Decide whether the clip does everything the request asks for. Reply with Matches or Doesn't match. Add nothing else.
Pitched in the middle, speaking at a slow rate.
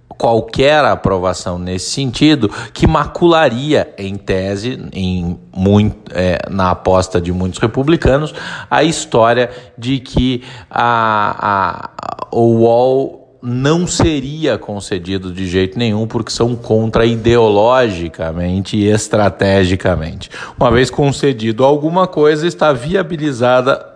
Doesn't match